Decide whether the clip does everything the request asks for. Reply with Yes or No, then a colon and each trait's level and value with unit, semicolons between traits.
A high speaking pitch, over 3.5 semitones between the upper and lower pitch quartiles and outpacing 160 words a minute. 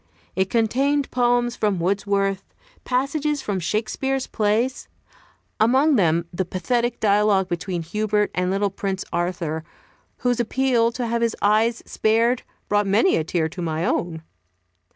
No: high, 210 Hz; average, 4.4 semitones; slow, 135 wpm